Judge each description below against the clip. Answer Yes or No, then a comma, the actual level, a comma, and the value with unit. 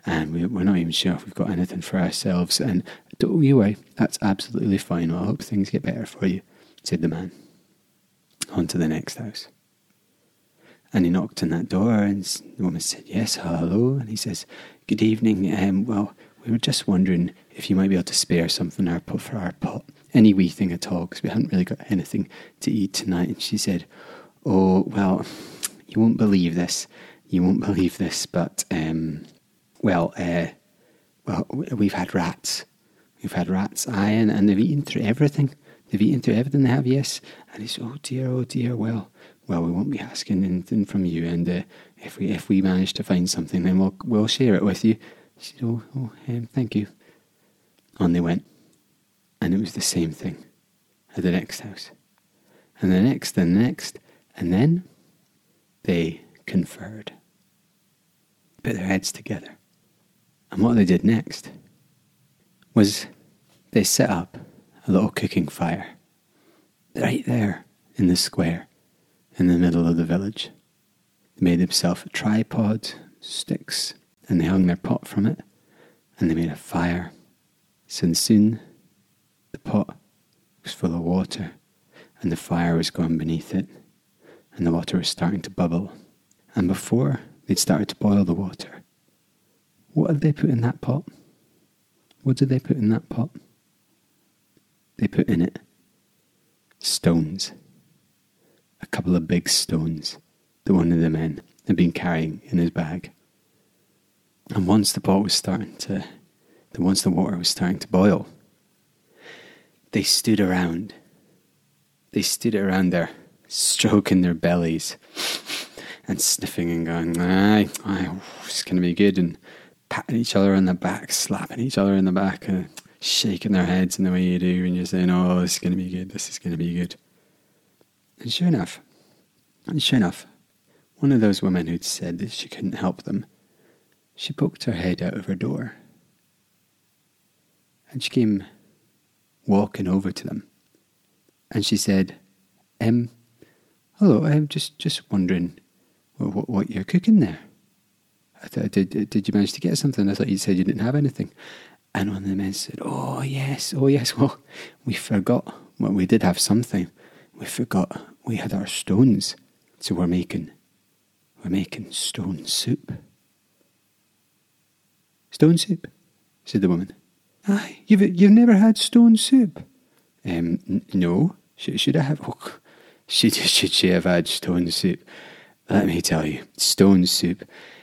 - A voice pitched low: Yes, low, 100 Hz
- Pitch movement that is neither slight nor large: Yes, average, 5.0 semitones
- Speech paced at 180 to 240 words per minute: No, average, 170 wpm